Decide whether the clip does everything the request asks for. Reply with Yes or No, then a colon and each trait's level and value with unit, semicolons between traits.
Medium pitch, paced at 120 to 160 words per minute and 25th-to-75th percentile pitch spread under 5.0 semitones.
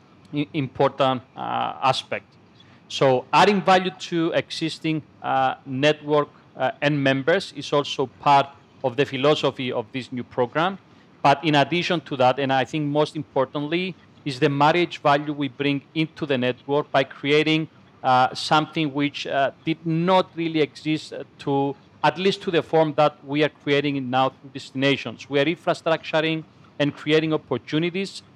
Yes: medium, 145 Hz; average, 150 wpm; average, 2.7 semitones